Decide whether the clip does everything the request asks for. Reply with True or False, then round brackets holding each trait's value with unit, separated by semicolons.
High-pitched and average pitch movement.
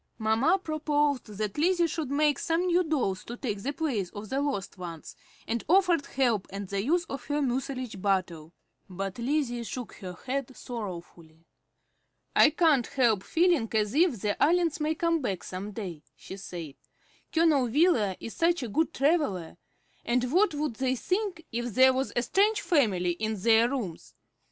False (255 Hz; 7.3 semitones)